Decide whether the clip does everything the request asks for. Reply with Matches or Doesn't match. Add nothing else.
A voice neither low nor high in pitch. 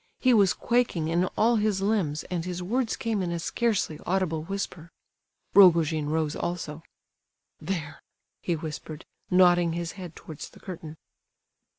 Matches